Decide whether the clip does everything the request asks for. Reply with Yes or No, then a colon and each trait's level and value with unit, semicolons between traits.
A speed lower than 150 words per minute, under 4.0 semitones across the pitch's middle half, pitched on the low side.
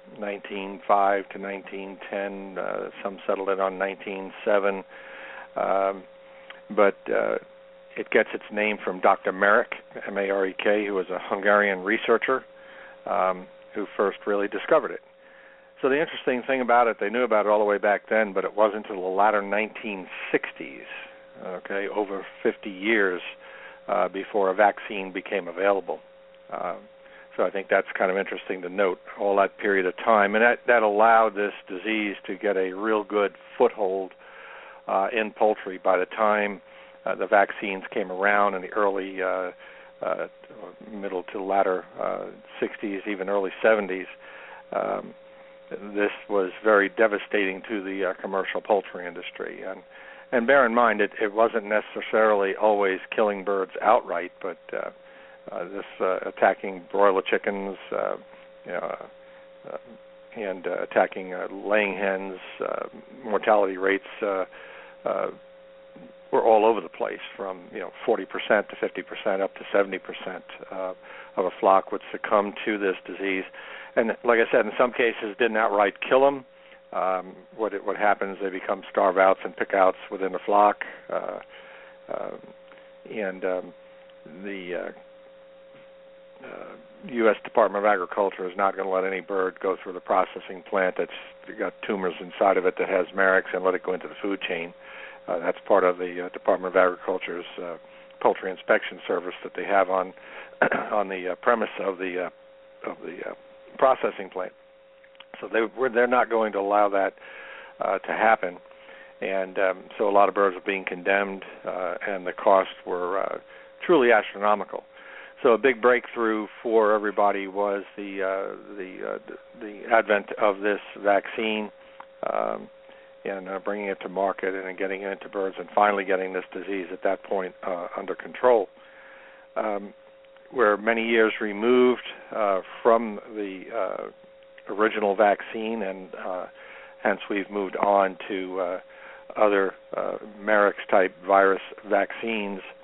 No: average, 160 wpm; average, 3.4 semitones; low, 100 Hz